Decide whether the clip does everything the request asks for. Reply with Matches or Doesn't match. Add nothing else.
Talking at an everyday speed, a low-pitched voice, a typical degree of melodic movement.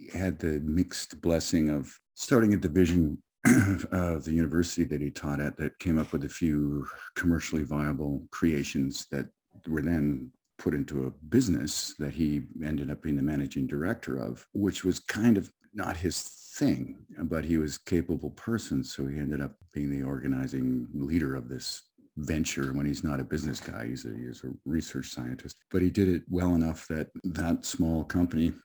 Matches